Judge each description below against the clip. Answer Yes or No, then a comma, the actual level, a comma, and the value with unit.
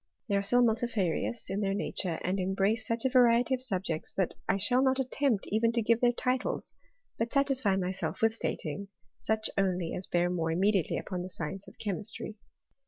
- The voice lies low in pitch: No, high, 205 Hz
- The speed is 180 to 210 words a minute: Yes, average, 185 wpm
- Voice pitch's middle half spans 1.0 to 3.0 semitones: No, average, 4.2 semitones